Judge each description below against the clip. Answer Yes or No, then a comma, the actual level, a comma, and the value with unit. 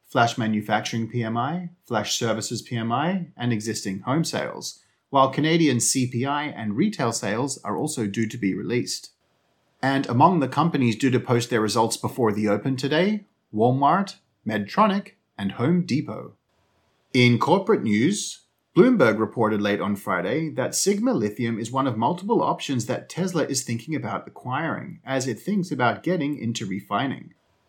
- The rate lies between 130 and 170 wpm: Yes, average, 150 wpm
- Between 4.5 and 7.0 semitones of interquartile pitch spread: Yes, average, 5.0 semitones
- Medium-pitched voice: No, low, 125 Hz